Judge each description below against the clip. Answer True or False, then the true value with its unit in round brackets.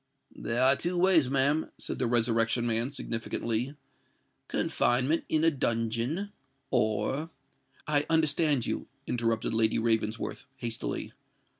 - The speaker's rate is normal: False (115 wpm)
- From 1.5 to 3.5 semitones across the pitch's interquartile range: False (4.8 semitones)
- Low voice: True (125 Hz)